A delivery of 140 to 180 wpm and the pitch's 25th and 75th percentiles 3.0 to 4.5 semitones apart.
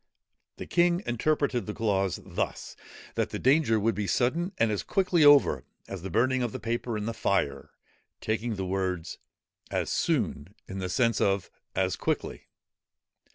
No: average, 160 wpm; average, 5.1 semitones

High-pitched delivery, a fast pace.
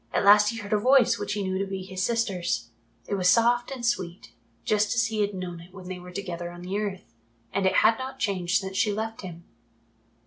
Yes: high, 200 Hz; fast, 235 wpm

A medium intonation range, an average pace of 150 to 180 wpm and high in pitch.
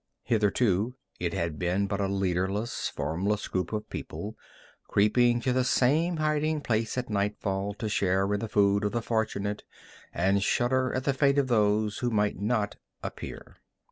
No: average, 3.7 semitones; average, 165 wpm; low, 105 Hz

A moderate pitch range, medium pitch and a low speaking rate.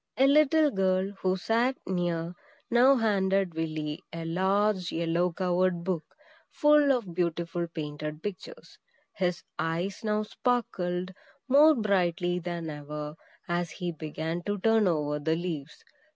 Yes: average, 4.1 semitones; medium, 180 Hz; slow, 130 wpm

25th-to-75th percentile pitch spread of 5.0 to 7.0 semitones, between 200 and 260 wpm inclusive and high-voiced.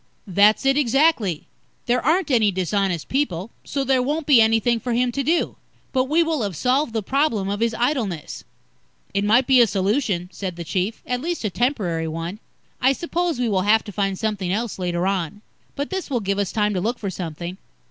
Yes: wide, 5.6 semitones; fast, 205 wpm; high, 220 Hz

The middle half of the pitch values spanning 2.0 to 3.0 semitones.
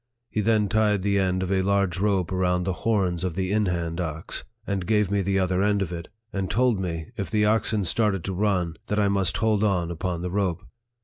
Yes: narrow, 2.5 semitones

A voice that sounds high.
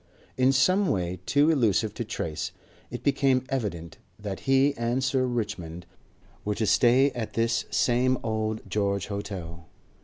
No: low, 115 Hz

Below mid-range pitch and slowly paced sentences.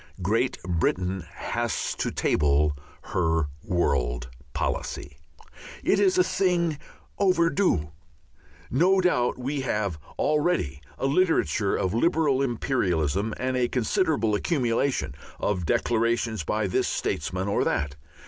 Yes: low, 115 Hz; slow, 110 wpm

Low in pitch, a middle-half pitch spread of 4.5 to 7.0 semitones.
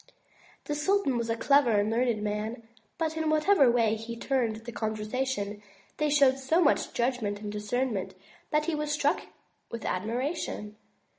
No: high, 240 Hz; average, 5.2 semitones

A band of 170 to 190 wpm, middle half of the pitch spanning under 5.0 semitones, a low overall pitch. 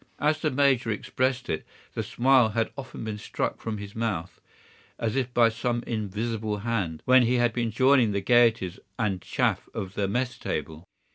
Yes: average, 180 wpm; average, 3.3 semitones; low, 115 Hz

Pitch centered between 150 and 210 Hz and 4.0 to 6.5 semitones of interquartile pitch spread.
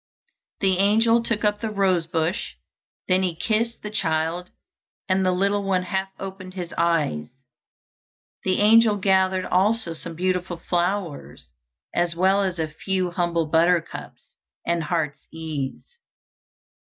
No: medium, 185 Hz; average, 2.9 semitones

